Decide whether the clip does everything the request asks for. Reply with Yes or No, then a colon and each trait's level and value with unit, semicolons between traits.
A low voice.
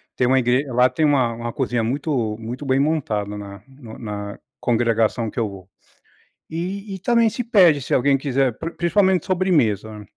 Yes: low, 130 Hz